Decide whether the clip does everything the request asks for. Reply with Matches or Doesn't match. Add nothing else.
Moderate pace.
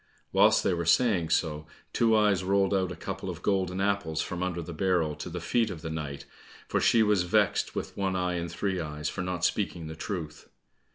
Doesn't match